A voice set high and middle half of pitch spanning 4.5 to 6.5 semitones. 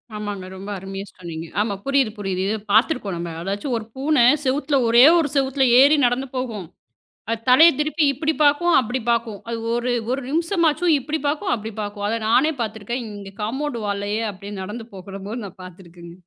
Yes: high, 230 Hz; wide, 5.5 semitones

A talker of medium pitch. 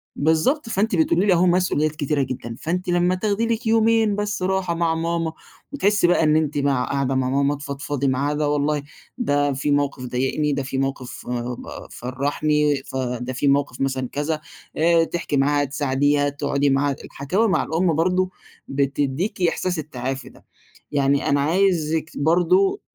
Yes: medium, 150 Hz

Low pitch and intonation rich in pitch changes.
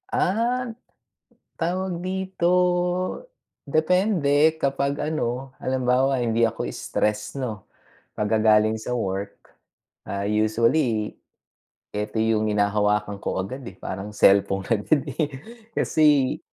Yes: low, 120 Hz; wide, 6.4 semitones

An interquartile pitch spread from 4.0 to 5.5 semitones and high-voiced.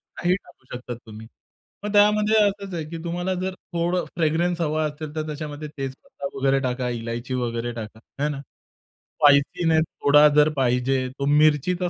No: average, 4.6 semitones; medium, 150 Hz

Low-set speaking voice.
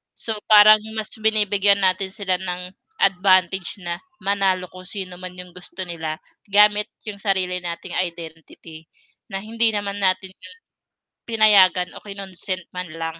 No: high, 190 Hz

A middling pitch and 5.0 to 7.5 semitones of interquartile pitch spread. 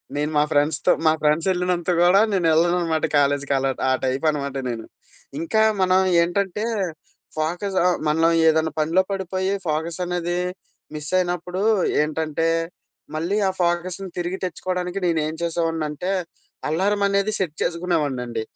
No: medium, 170 Hz; average, 2.8 semitones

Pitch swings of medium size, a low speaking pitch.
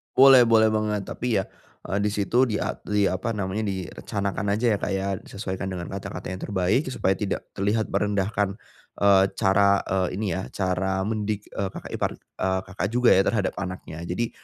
No: narrow, 2.1 semitones; low, 100 Hz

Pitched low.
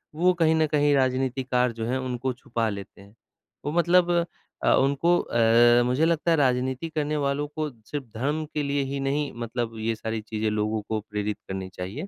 Yes: low, 130 Hz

